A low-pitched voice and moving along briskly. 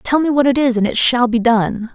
No: high, 245 Hz; fast, 310 wpm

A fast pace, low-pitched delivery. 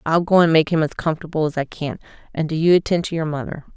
No: fast, 270 wpm; medium, 160 Hz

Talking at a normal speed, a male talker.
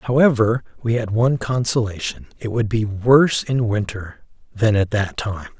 Yes: average, 150 wpm; male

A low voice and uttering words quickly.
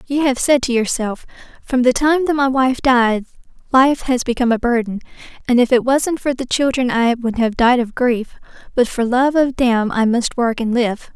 No: high, 245 Hz; fast, 215 wpm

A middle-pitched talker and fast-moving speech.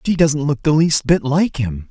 Yes: medium, 150 Hz; fast, 250 wpm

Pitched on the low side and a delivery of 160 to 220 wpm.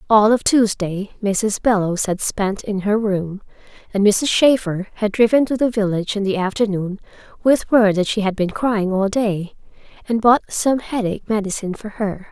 No: high, 210 Hz; average, 180 wpm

